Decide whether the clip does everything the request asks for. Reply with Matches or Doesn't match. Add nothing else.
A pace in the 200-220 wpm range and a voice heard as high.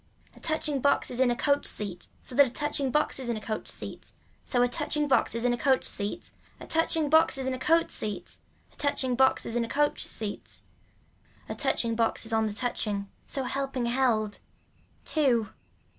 Matches